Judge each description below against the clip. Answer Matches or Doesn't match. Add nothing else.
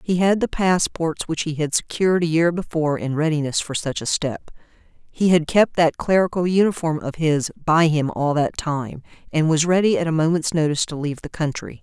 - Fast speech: Matches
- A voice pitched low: Doesn't match